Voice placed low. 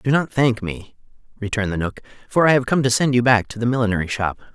Yes: low, 115 Hz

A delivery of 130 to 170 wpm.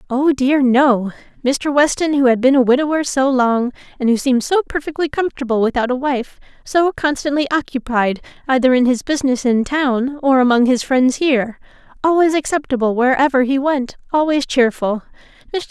Yes: average, 160 wpm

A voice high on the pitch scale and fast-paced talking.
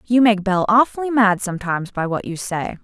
Yes: high, 205 Hz; fast, 210 wpm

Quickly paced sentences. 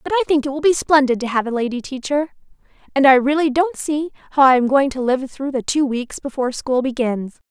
Yes: fast, 230 wpm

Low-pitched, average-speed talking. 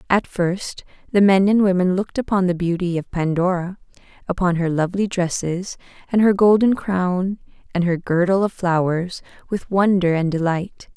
No: medium, 185 Hz; average, 160 wpm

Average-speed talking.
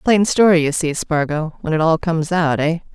No: fast, 225 wpm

